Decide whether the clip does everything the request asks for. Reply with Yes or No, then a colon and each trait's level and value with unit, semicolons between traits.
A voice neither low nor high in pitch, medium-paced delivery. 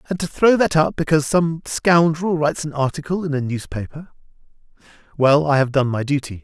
Yes: medium, 150 Hz; average, 175 wpm